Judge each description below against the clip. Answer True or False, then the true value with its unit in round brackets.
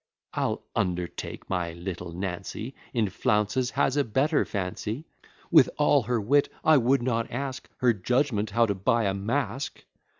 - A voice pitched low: True (115 Hz)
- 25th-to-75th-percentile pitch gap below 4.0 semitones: False (5.3 semitones)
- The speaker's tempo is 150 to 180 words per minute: True (155 wpm)